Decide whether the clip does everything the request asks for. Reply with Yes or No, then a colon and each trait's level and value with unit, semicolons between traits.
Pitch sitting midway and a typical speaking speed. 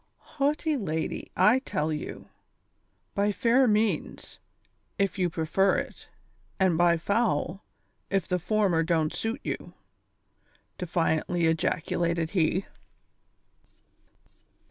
No: medium, 180 Hz; slow, 105 wpm